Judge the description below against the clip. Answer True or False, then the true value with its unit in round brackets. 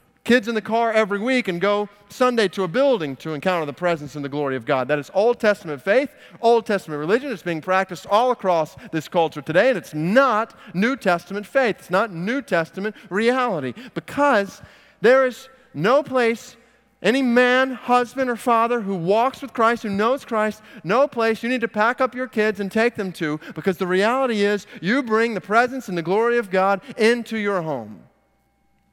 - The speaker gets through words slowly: False (195 wpm)